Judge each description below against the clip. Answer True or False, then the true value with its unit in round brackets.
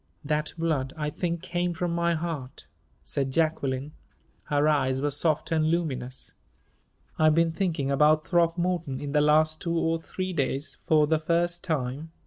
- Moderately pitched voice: True (155 Hz)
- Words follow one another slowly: False (155 wpm)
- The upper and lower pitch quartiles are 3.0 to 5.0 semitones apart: False (2.6 semitones)